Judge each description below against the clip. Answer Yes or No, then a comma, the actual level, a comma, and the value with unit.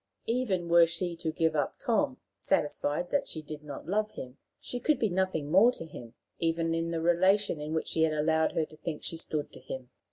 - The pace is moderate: No, fast, 220 wpm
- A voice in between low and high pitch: Yes, medium, 165 Hz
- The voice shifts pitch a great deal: No, average, 3.4 semitones